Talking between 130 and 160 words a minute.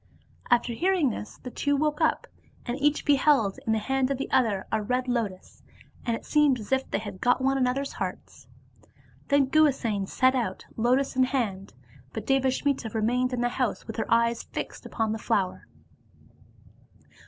No: average, 175 wpm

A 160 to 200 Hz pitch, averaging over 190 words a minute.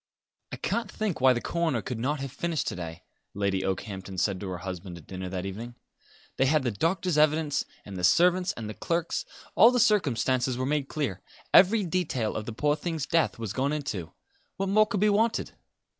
No: low, 135 Hz; fast, 205 wpm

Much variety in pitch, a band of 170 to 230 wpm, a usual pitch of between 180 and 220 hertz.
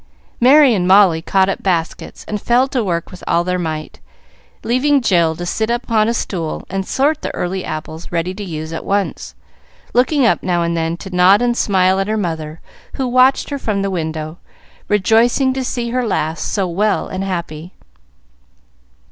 Yes: wide, 5.8 semitones; average, 180 wpm; high, 190 Hz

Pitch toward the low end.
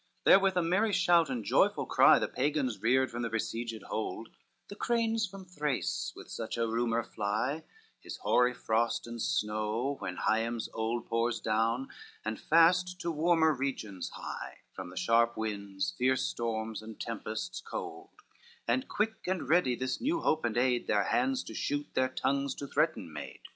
Yes: low, 120 Hz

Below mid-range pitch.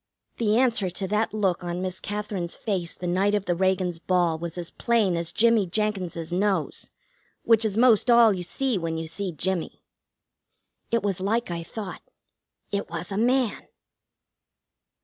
No: high, 190 Hz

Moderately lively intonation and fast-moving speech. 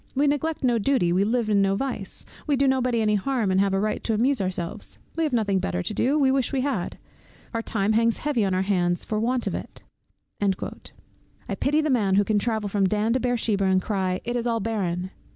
Yes: average, 4.6 semitones; fast, 235 wpm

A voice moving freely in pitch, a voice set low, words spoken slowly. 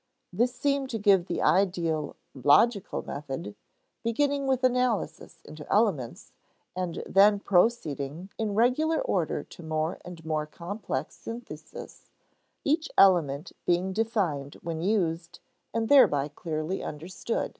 No: wide, 6.4 semitones; medium, 185 Hz; slow, 120 wpm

